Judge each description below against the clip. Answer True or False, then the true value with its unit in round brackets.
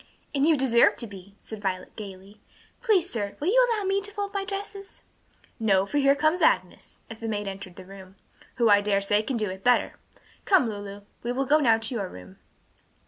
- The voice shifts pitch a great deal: True (7.7 semitones)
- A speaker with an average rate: False (210 wpm)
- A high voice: True (225 Hz)